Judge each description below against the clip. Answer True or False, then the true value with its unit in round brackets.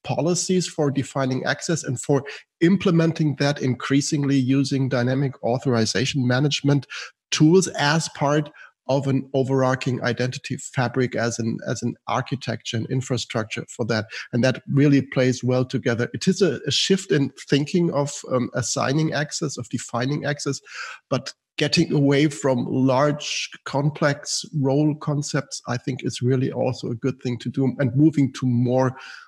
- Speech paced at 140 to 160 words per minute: True (150 wpm)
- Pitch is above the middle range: False (135 Hz)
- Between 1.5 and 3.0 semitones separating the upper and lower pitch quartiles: True (2.6 semitones)